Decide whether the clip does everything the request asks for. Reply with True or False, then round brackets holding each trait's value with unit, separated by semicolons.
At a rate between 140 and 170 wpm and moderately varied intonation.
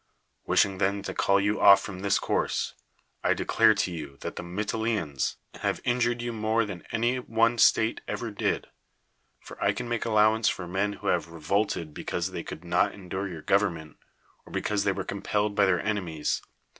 False (185 wpm; 3.7 semitones)